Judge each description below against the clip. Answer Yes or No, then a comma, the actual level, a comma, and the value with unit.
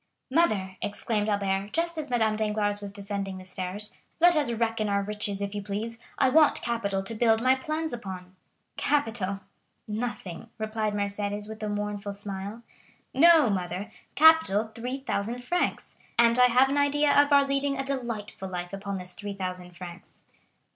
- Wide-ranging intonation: No, average, 4.1 semitones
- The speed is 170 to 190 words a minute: No, average, 155 wpm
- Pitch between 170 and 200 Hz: No, high, 215 Hz